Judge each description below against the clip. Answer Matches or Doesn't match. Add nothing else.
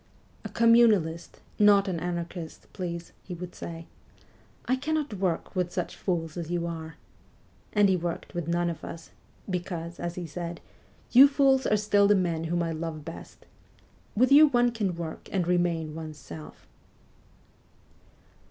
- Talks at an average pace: Matches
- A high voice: Doesn't match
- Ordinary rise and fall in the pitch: Matches